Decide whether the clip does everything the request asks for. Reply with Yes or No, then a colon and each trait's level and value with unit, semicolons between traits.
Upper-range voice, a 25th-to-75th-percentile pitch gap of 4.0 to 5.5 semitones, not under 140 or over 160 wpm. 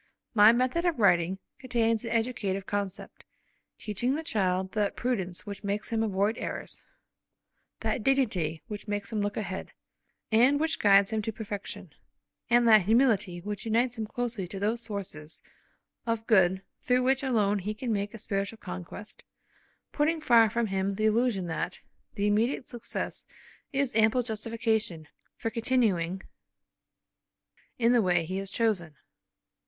No: high, 215 Hz; average, 3.3 semitones; average, 150 wpm